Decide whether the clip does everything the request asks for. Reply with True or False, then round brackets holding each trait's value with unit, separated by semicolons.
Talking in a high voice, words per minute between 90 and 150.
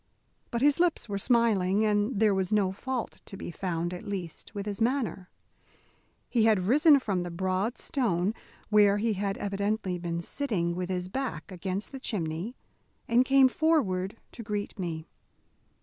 False (205 Hz; 165 wpm)